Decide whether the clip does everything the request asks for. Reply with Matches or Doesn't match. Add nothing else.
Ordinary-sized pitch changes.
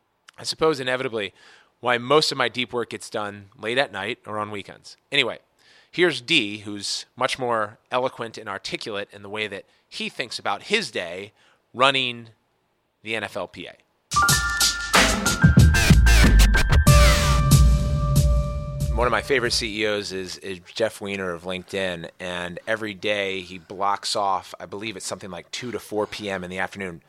Matches